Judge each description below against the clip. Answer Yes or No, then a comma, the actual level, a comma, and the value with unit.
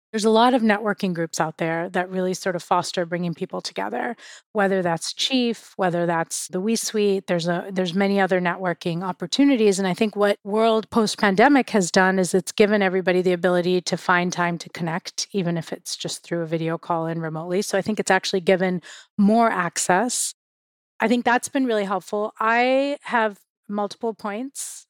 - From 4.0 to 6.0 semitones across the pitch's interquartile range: No, average, 3.4 semitones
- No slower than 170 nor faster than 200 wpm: Yes, average, 190 wpm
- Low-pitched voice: No, high, 190 Hz